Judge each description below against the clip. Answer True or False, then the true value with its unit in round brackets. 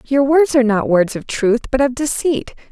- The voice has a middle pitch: False (255 Hz)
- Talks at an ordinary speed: False (220 wpm)